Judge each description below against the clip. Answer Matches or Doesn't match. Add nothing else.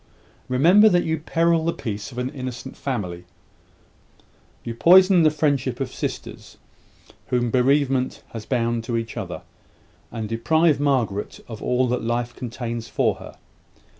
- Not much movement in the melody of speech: Doesn't match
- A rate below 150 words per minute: Matches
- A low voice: Matches